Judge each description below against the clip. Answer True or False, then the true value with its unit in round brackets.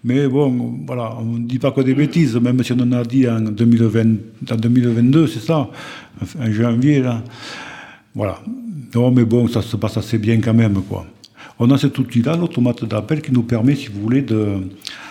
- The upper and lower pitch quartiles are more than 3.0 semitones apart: False (2.7 semitones)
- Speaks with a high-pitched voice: False (120 Hz)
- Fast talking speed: False (200 wpm)